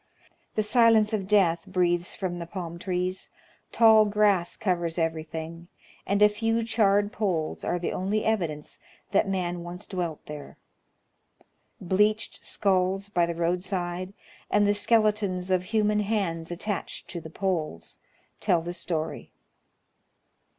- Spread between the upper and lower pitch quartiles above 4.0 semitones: No, average, 3.3 semitones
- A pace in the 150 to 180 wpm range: No, slow, 135 wpm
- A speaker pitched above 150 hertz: Yes, medium, 185 Hz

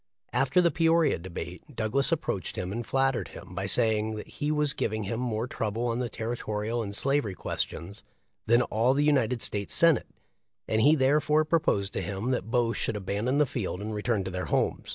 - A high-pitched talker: No, low, 115 Hz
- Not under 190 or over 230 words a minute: Yes, average, 195 wpm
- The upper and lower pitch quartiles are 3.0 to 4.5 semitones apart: No, average, 4.9 semitones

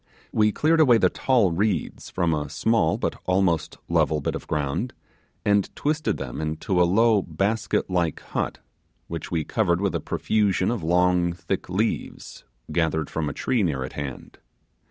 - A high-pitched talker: No, very low, 90 Hz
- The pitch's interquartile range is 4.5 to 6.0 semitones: Yes, average, 5.2 semitones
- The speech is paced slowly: No, average, 165 wpm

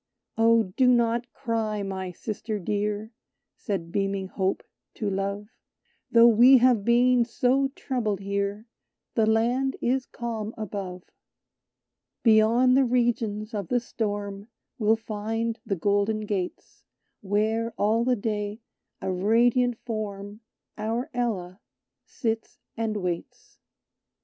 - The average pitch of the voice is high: Yes, high, 220 Hz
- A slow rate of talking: Yes, slow, 115 wpm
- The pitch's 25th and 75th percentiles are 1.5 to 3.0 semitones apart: Yes, average, 2.7 semitones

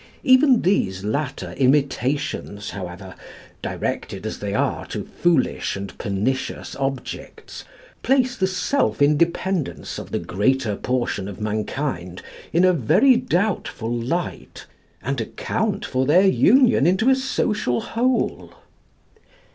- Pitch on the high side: No, medium, 140 Hz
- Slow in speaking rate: Yes, slow, 115 wpm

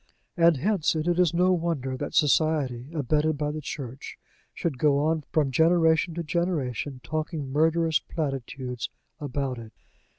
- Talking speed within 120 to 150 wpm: Yes, average, 140 wpm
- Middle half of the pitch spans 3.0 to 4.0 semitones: Yes, average, 3.4 semitones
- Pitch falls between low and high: Yes, medium, 155 Hz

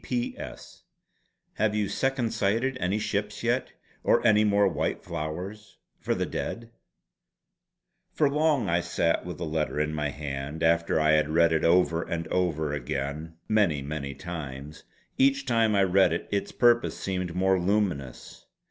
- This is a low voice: Yes, very low, 90 Hz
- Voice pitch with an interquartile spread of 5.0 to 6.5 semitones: Yes, wide, 5.5 semitones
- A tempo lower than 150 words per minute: No, average, 155 wpm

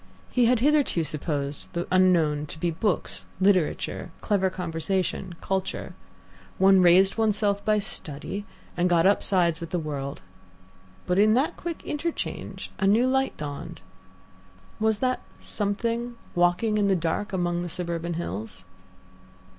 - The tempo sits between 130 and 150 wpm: Yes, slow, 135 wpm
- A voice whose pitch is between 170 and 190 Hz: Yes, medium, 185 Hz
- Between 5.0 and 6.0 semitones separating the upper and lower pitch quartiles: No, average, 4.0 semitones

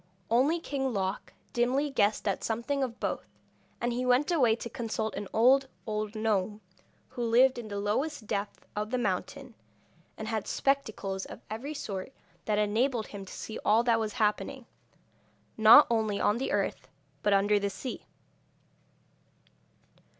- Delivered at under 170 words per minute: Yes, average, 155 wpm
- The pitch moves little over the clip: No, average, 3.4 semitones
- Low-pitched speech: No, high, 225 Hz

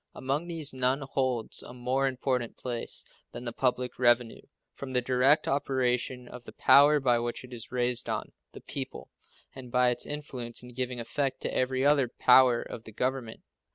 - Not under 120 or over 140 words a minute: No, average, 180 wpm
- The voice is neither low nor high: No, low, 125 Hz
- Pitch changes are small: Yes, narrow, 1.6 semitones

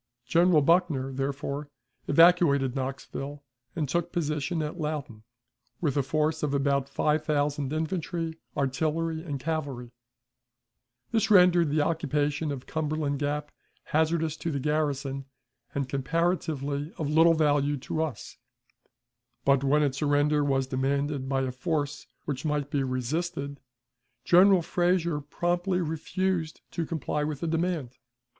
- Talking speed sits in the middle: No, slow, 130 wpm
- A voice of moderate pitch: Yes, medium, 150 Hz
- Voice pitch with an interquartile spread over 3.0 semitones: No, average, 2.7 semitones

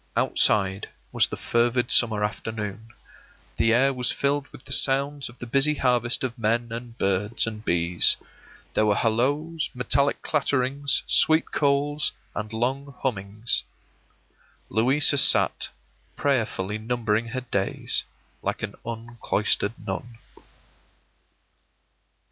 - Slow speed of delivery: Yes, slow, 115 wpm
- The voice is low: Yes, low, 120 Hz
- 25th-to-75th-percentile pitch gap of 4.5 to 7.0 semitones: No, average, 4.1 semitones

